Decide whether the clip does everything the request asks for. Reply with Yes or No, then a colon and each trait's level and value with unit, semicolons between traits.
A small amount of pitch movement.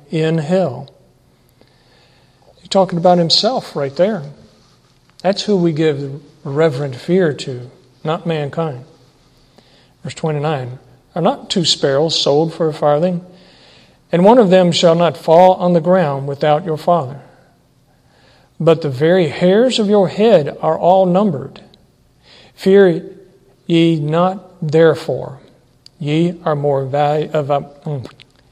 No: average, 4.2 semitones